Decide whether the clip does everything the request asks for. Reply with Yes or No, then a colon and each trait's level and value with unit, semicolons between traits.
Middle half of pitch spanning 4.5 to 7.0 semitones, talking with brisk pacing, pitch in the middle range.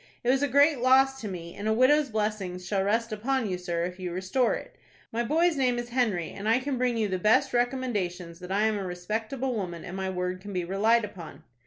No: wide, 5.4 semitones; fast, 235 wpm; high, 215 Hz